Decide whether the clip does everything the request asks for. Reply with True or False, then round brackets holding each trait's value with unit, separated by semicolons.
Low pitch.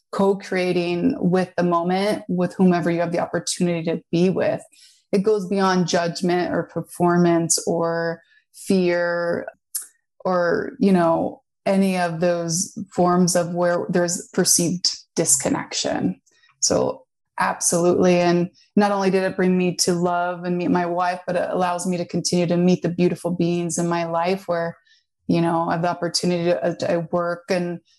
False (175 Hz)